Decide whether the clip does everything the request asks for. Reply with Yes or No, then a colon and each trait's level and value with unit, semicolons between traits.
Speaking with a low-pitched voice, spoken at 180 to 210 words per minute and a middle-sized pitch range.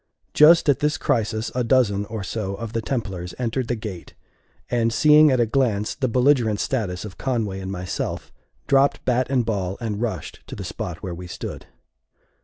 Yes: low, 115 Hz; average, 185 wpm; average, 4.5 semitones